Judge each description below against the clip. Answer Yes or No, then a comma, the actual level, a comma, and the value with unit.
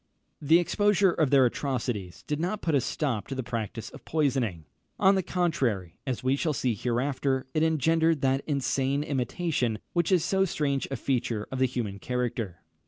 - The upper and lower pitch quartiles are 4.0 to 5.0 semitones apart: Yes, average, 4.7 semitones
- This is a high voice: No, low, 135 Hz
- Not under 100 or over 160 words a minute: No, average, 175 wpm